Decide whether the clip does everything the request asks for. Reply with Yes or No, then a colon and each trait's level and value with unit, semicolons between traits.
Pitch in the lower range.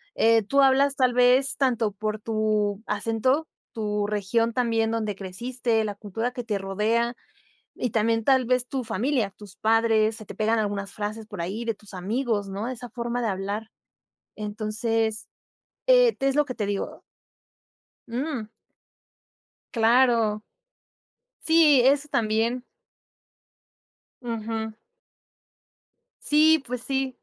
No: high, 225 Hz